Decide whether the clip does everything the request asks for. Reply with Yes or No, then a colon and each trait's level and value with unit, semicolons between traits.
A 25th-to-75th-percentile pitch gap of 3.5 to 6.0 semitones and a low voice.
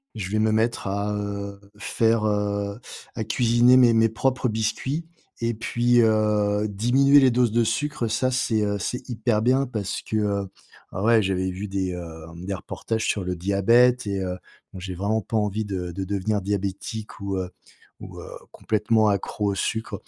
No: average, 2.8 semitones; low, 105 Hz